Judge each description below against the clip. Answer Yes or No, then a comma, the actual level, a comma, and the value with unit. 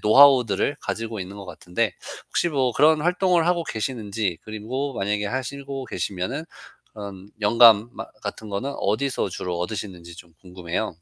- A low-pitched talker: Yes, low, 110 Hz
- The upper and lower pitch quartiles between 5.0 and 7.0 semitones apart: Yes, wide, 5.5 semitones